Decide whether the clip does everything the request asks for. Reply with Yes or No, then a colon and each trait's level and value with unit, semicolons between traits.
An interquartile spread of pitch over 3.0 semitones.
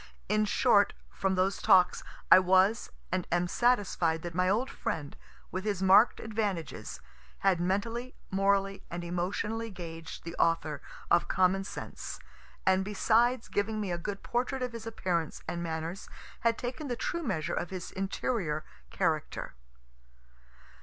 Yes: average, 4.1 semitones